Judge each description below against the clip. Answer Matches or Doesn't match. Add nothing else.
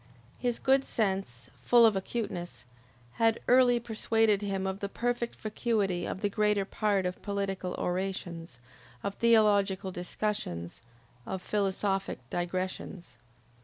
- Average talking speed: Doesn't match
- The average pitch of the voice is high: Matches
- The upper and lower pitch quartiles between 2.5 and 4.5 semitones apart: Matches